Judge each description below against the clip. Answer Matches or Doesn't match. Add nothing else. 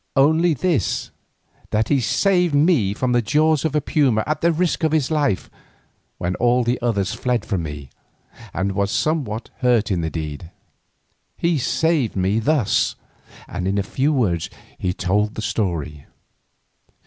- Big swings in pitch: Matches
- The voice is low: Matches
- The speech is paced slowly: Doesn't match